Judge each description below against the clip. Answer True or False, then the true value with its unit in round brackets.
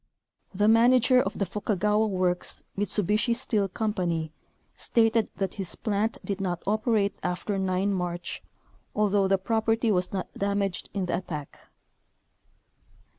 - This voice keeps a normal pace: False (125 wpm)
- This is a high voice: True (200 Hz)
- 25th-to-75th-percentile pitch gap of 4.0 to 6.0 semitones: False (2.8 semitones)